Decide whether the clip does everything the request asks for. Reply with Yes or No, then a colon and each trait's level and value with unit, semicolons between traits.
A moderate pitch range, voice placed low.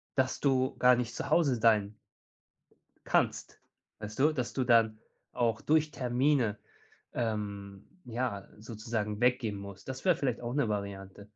Yes: average, 3.6 semitones; low, 115 Hz